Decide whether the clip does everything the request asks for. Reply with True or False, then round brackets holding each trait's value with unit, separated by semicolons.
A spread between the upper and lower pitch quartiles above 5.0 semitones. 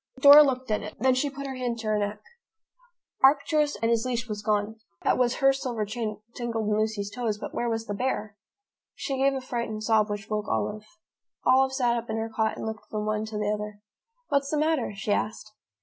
False (3.5 semitones)